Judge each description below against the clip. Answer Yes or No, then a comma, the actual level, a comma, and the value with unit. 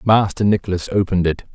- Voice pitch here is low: Yes, very low, 95 Hz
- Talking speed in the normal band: Yes, average, 155 wpm